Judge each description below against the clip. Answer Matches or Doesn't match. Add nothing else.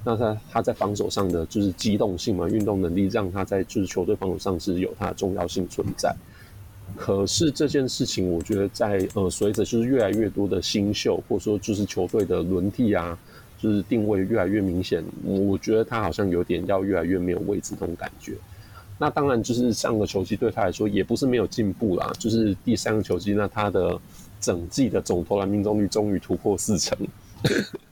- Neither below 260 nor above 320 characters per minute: Matches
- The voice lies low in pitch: Matches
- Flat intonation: Matches